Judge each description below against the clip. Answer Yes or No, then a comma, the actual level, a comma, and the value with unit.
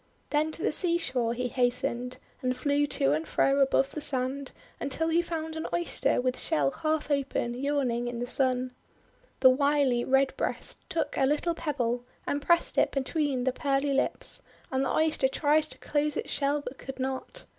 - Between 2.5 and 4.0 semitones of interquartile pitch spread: Yes, average, 2.9 semitones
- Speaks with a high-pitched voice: Yes, very high, 275 Hz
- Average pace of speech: Yes, average, 175 wpm